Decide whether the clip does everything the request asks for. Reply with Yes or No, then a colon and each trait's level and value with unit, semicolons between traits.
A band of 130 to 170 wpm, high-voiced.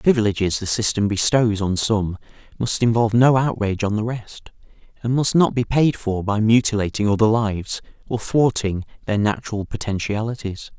No: average, 160 wpm; low, 110 Hz